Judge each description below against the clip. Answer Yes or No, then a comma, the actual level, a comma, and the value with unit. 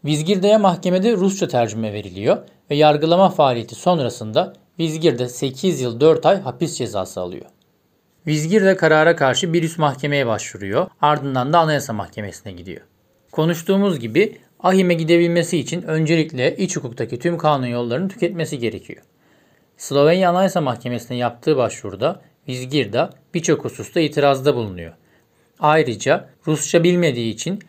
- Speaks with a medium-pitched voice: Yes, medium, 155 Hz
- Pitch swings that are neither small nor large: No, wide, 5.8 semitones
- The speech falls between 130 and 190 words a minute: No, average, 120 wpm